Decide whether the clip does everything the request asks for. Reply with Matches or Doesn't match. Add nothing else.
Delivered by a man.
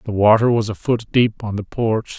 Matches